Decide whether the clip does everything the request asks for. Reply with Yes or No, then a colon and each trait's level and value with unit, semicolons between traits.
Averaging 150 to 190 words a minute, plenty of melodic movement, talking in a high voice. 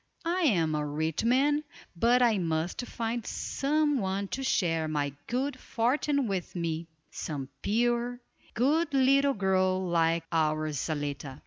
No: slow, 135 wpm; wide, 8.0 semitones; high, 195 Hz